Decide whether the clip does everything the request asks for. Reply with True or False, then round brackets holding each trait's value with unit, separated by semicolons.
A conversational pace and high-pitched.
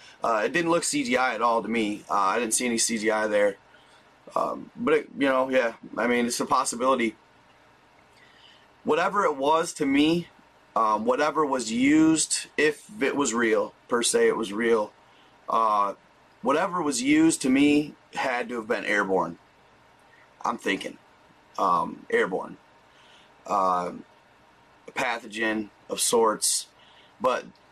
False (145 wpm; 140 Hz)